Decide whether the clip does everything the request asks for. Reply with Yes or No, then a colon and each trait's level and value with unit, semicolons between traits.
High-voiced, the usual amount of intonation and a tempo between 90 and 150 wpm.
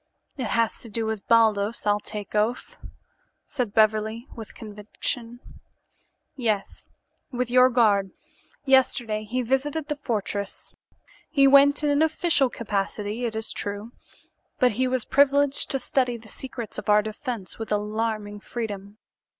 Yes: high, 230 Hz; average, 3.5 semitones; average, 140 wpm